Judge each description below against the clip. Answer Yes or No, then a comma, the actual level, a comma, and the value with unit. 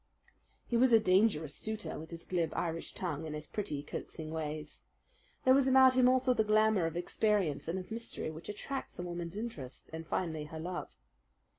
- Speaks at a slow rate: No, average, 185 wpm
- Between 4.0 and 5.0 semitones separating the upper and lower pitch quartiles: No, wide, 5.5 semitones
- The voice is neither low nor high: Yes, medium, 175 Hz